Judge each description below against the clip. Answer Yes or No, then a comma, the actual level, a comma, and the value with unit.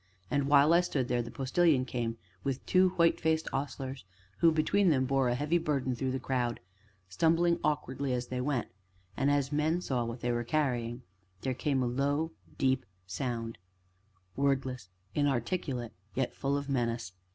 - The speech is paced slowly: No, average, 165 wpm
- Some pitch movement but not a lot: Yes, average, 3.3 semitones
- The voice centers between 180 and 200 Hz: No, low, 135 Hz